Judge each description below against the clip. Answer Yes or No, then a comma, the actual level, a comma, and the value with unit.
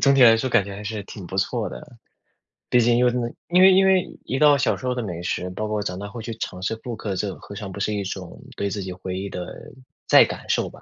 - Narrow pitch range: No, average, 4.4 semitones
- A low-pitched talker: Yes, low, 105 Hz